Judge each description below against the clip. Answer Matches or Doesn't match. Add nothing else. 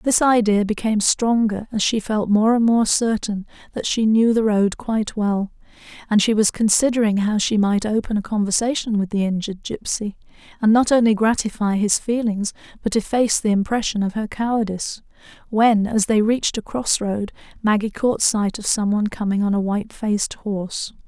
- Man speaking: Doesn't match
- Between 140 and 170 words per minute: Doesn't match